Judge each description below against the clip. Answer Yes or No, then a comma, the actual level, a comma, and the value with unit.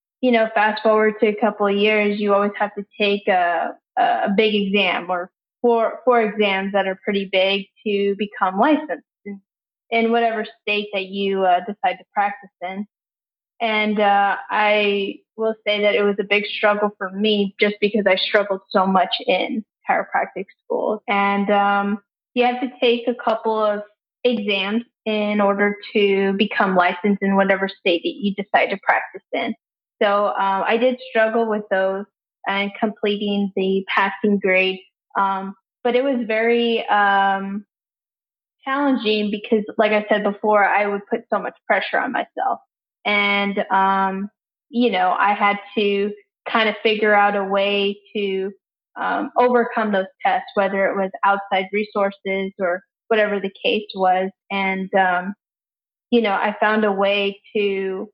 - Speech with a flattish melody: Yes, narrow, 2.1 semitones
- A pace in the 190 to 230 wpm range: No, average, 160 wpm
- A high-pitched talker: Yes, high, 205 Hz